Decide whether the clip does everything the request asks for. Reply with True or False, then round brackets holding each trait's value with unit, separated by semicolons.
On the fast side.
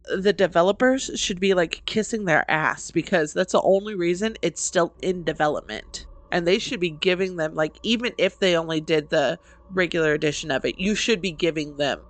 False (195 wpm)